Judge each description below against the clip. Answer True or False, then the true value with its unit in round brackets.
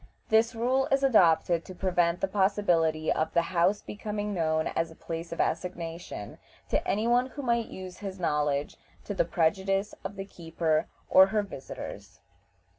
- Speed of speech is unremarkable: True (165 wpm)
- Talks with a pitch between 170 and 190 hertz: True (185 Hz)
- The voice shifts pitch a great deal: False (4.0 semitones)